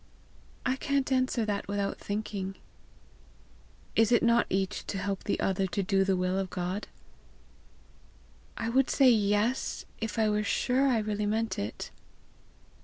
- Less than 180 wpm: Yes, average, 150 wpm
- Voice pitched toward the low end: No, high, 210 Hz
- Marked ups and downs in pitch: No, average, 3.4 semitones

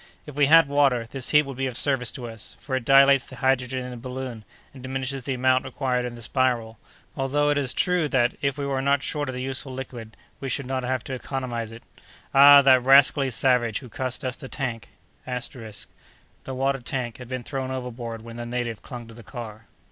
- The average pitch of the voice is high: No, low, 130 Hz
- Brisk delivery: Yes, fast, 215 wpm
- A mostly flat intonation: Yes, narrow, 2.1 semitones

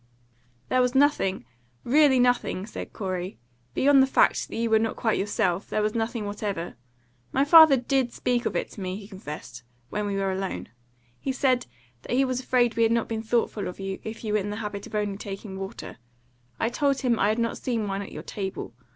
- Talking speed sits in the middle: No, fast, 215 wpm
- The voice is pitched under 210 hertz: No, high, 220 Hz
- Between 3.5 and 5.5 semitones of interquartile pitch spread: Yes, average, 4.0 semitones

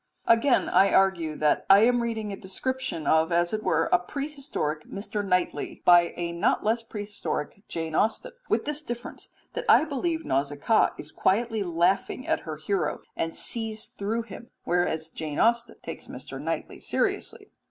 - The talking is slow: No, average, 165 wpm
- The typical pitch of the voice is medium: No, high, 200 Hz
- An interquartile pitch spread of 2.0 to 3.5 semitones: No, wide, 5.6 semitones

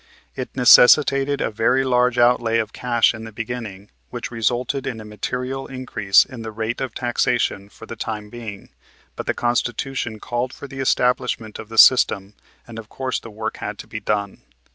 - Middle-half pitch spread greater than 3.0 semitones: No, narrow, 2.4 semitones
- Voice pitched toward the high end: No, low, 120 Hz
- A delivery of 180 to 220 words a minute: Yes, average, 185 wpm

